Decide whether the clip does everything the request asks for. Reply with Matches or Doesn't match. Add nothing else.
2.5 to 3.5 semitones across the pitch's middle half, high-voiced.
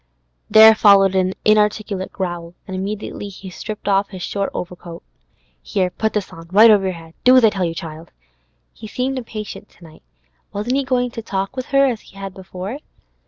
Matches